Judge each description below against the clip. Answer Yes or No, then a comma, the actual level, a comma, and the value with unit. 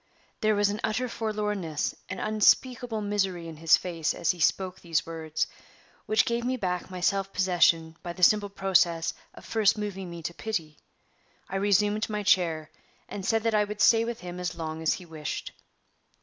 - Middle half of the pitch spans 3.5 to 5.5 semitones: Yes, average, 3.9 semitones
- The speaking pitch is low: No, high, 190 Hz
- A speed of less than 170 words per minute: No, average, 185 wpm